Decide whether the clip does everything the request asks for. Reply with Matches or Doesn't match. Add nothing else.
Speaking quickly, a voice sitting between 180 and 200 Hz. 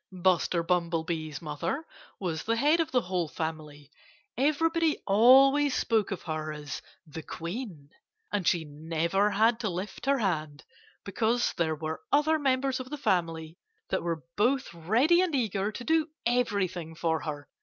Doesn't match